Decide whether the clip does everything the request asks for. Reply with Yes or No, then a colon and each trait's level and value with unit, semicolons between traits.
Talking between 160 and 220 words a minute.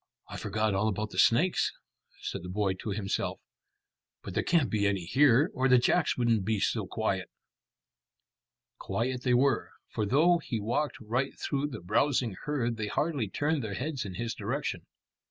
Yes: average, 170 wpm